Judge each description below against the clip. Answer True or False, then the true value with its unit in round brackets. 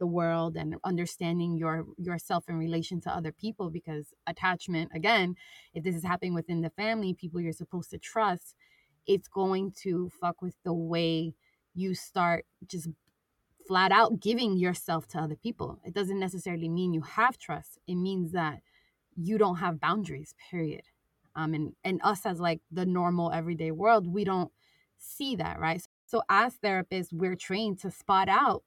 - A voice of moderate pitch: True (180 Hz)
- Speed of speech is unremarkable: True (170 wpm)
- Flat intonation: True (2.3 semitones)